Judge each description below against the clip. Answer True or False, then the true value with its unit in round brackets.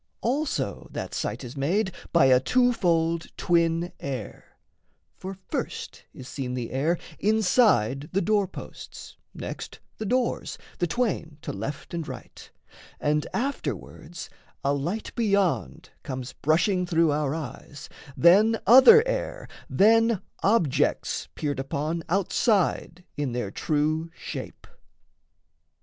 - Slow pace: True (120 wpm)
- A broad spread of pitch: True (6.6 semitones)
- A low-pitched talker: False (170 Hz)